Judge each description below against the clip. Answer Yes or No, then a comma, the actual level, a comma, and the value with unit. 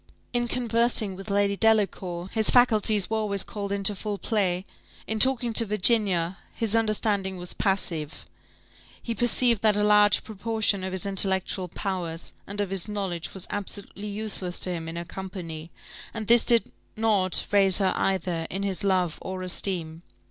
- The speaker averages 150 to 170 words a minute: Yes, average, 160 wpm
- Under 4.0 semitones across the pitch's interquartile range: Yes, average, 2.7 semitones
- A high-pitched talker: Yes, high, 200 Hz